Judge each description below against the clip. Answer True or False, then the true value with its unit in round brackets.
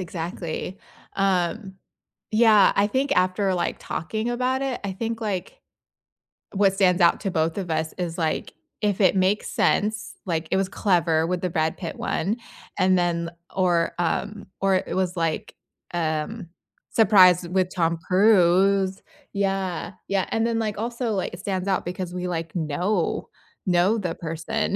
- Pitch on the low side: False (185 Hz)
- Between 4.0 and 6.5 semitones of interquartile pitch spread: False (2.9 semitones)